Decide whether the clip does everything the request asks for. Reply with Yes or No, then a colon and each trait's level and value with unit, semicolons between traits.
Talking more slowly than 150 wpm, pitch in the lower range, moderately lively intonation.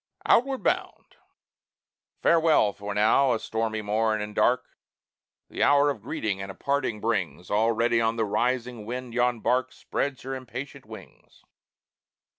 Yes: average, 140 wpm; low, 115 Hz; average, 3.3 semitones